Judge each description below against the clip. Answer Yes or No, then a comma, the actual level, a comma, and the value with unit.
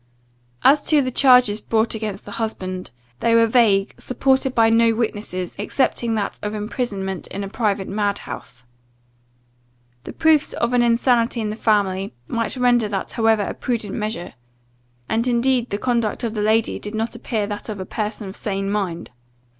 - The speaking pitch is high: Yes, high, 220 Hz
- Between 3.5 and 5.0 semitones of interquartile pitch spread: No, narrow, 2.6 semitones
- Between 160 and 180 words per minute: Yes, average, 170 wpm